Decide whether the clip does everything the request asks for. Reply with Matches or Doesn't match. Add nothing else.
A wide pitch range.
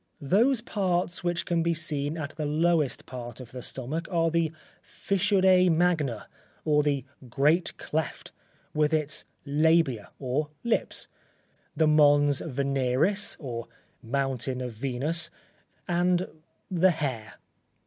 Doesn't match